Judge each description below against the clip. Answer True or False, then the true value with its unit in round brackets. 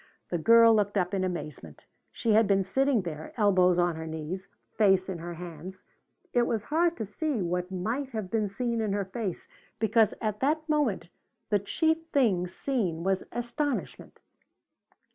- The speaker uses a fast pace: False (165 wpm)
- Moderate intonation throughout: True (4.6 semitones)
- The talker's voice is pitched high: True (205 Hz)